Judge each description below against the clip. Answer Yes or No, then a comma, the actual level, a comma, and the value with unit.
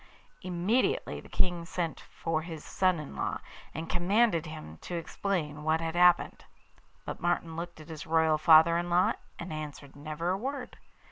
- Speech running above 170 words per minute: No, average, 165 wpm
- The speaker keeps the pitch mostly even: Yes, narrow, 2.2 semitones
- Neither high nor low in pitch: Yes, medium, 170 Hz